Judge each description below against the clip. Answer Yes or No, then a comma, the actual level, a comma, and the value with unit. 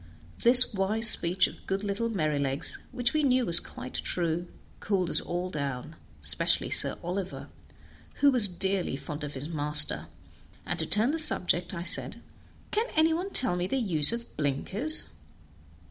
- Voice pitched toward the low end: No, medium, 185 Hz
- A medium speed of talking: Yes, average, 160 wpm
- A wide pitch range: Yes, wide, 7.3 semitones